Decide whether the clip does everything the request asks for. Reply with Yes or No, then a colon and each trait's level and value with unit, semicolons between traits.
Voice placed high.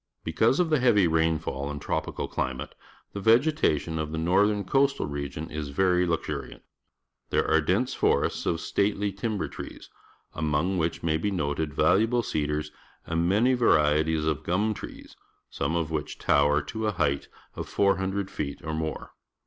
No: very low, 85 Hz